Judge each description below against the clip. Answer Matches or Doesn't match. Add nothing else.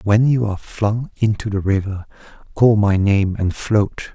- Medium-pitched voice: Doesn't match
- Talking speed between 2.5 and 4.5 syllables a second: Matches